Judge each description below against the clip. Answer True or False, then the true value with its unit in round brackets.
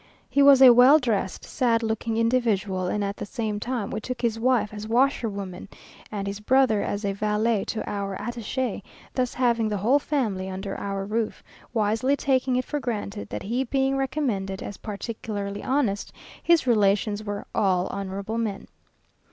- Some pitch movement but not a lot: True (3.9 semitones)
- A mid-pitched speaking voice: False (220 Hz)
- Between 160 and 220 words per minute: True (165 wpm)